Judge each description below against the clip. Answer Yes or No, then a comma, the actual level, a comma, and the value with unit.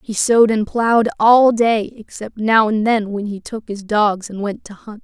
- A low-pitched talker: No, high, 215 Hz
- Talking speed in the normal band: No, fast, 225 wpm